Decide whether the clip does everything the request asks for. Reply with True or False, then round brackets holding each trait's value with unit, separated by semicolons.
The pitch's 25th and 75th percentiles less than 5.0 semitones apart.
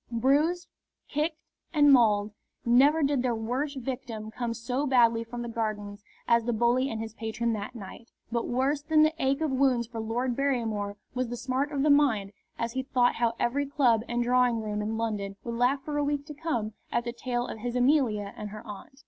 True (3.5 semitones)